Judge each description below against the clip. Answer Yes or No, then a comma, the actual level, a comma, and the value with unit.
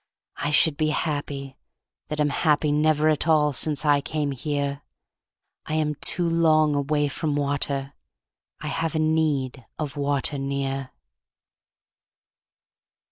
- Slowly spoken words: Yes, slow, 130 wpm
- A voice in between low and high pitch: Yes, medium, 145 Hz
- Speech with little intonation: Yes, narrow, 1.7 semitones